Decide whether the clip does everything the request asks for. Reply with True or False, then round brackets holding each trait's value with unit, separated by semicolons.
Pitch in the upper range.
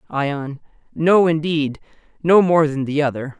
False (150 Hz)